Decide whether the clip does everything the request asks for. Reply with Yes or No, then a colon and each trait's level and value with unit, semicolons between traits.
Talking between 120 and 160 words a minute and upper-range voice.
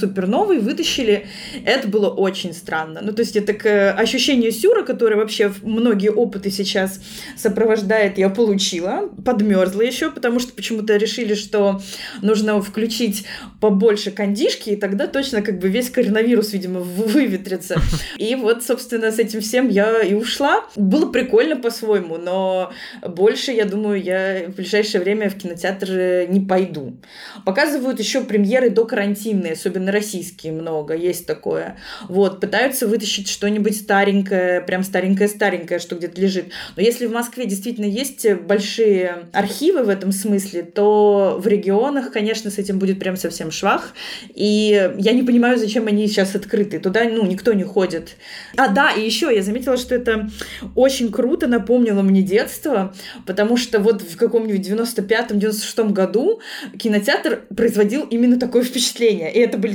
Yes: average, 150 wpm; high, 210 Hz